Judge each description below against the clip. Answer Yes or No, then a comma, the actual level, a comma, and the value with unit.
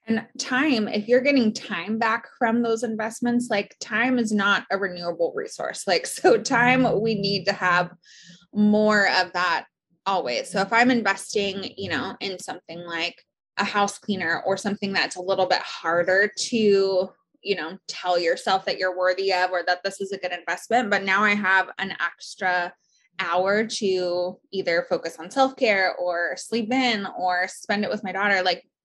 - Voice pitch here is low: No, high, 195 Hz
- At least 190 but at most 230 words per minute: No, average, 180 wpm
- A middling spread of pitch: Yes, average, 3.4 semitones